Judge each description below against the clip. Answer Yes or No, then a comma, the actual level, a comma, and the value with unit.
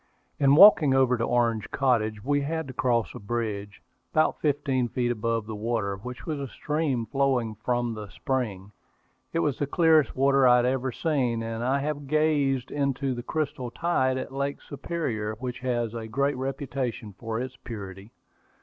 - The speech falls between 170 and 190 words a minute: Yes, average, 175 wpm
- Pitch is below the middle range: Yes, low, 130 Hz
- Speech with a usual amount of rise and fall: Yes, average, 3.3 semitones